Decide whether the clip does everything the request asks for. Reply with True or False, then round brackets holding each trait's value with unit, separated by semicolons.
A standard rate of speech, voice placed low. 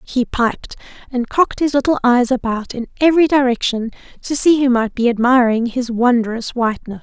False (170 wpm; 245 Hz)